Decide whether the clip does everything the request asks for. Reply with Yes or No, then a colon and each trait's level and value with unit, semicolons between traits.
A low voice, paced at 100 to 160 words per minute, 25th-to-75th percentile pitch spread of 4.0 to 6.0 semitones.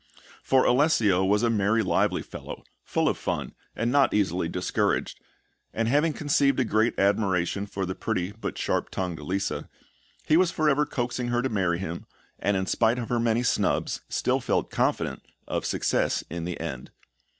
No: low, 110 Hz; average, 175 wpm; average, 4.8 semitones